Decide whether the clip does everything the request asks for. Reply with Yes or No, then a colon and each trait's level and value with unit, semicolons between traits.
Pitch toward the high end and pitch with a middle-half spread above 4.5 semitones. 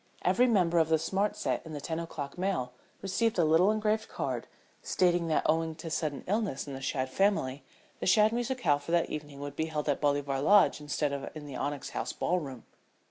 No: medium, 160 Hz; average, 4.9 semitones